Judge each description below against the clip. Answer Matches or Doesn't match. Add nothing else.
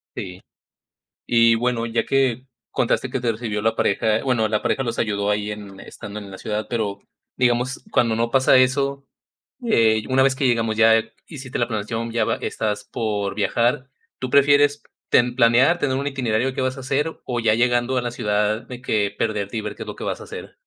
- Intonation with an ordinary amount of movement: Matches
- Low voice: Matches